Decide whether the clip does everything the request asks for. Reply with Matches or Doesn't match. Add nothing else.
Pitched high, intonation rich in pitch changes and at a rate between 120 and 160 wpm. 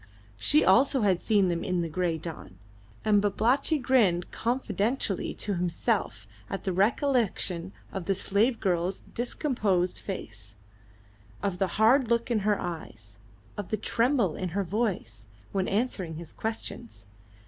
Doesn't match